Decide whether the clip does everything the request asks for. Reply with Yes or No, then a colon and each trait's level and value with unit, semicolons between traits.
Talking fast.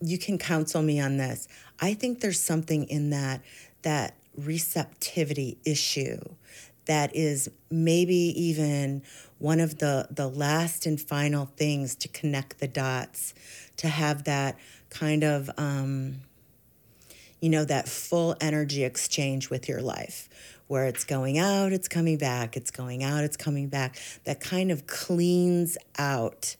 No: average, 145 wpm